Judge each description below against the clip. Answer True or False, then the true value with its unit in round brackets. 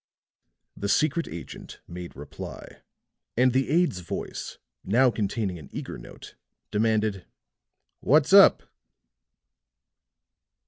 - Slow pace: True (95 wpm)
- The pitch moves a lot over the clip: True (6.7 semitones)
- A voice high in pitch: False (110 Hz)